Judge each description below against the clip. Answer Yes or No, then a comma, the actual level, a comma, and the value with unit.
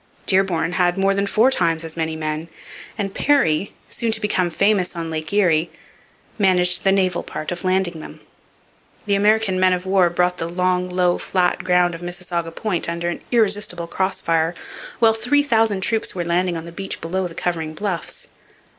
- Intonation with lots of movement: No, narrow, 2.6 semitones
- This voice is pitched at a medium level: Yes, medium, 180 Hz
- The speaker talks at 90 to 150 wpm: No, average, 180 wpm